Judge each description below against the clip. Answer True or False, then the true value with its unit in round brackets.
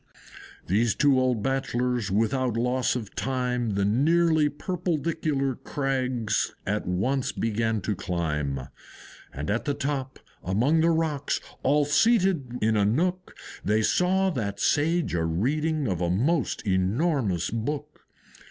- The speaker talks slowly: True (130 wpm)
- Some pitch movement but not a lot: False (6.1 semitones)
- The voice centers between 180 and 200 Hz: False (130 Hz)